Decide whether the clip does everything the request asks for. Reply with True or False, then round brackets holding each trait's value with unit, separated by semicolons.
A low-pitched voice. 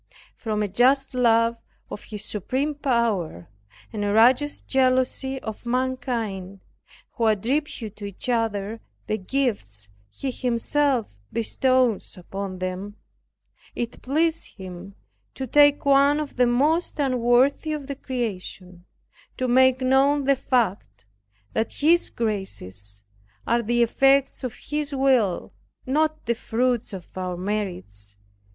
False (240 Hz)